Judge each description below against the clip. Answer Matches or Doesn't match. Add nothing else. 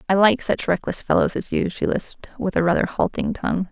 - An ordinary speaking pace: Doesn't match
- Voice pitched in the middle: Doesn't match